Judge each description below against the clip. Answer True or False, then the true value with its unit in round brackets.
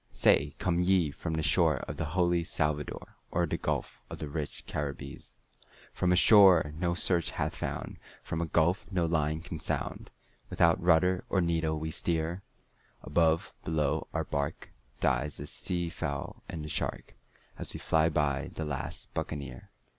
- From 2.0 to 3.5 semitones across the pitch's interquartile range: True (2.5 semitones)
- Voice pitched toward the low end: True (80 Hz)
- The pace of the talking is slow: False (165 wpm)